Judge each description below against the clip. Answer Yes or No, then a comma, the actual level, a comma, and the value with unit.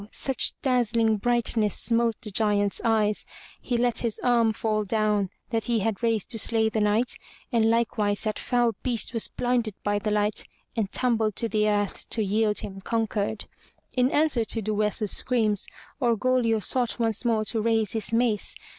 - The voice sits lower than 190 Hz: No, high, 225 Hz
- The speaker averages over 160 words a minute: Yes, average, 170 wpm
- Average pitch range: No, narrow, 2.0 semitones